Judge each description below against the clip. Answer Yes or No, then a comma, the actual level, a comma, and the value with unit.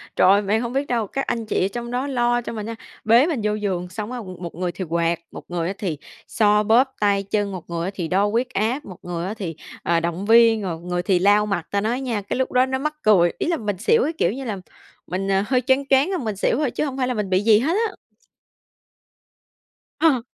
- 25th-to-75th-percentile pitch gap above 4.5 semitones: Yes, average, 5.1 semitones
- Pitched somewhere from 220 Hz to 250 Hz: No, high, 210 Hz